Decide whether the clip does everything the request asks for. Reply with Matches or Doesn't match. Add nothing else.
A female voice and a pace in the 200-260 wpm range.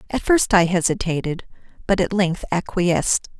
Doesn't match